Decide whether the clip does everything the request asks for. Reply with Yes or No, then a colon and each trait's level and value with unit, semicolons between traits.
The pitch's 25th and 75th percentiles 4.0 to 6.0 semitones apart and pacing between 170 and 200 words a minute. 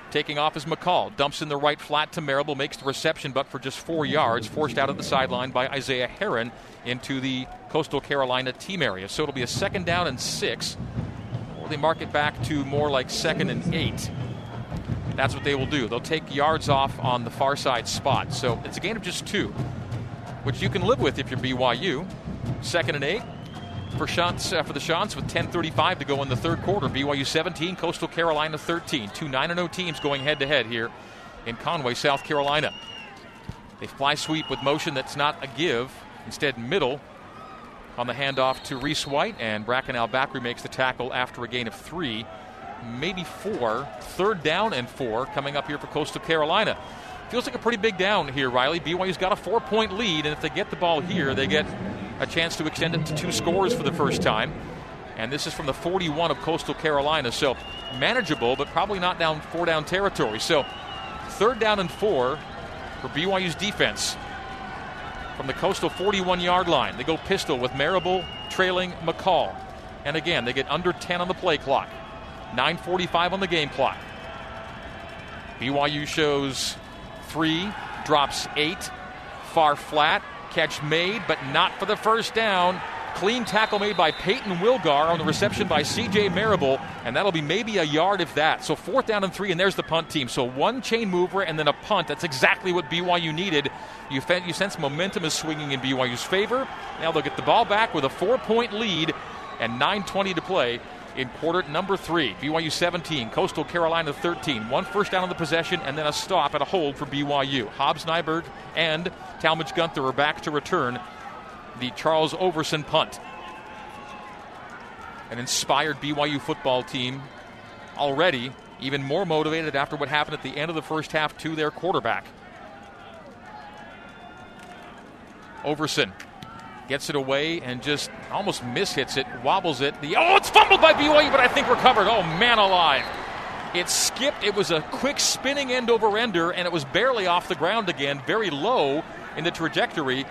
Yes: average, 4.7 semitones; average, 185 wpm